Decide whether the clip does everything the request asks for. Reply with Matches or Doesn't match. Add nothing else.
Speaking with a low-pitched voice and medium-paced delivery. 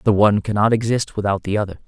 Doesn't match